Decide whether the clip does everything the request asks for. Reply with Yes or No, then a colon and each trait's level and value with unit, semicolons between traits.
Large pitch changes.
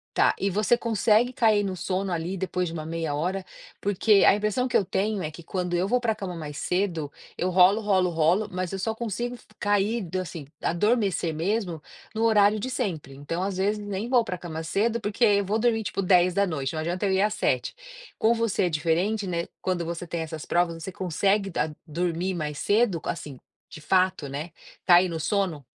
No: average, 3.7 semitones